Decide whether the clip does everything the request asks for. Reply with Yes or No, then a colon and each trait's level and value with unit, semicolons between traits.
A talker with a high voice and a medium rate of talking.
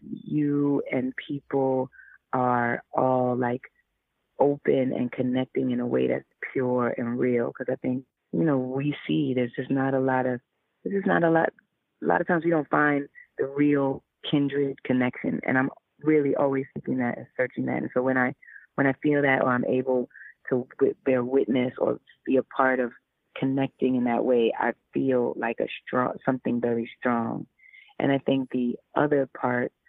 No: low, 130 Hz; average, 185 wpm